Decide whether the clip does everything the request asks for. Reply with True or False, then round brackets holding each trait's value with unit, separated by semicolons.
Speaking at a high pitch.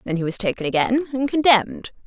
True (225 Hz)